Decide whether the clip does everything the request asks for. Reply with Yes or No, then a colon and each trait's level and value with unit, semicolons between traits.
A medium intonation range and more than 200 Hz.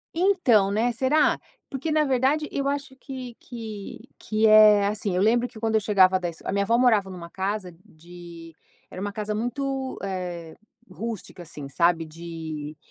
No: wide, 5.8 semitones; high, 210 Hz